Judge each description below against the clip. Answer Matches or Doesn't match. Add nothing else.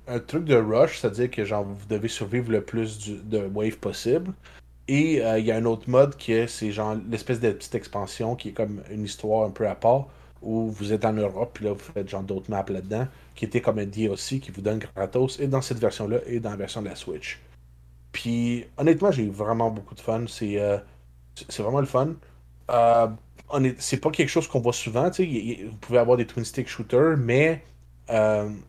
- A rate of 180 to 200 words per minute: Doesn't match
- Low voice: Matches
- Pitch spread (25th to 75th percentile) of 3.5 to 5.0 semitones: Doesn't match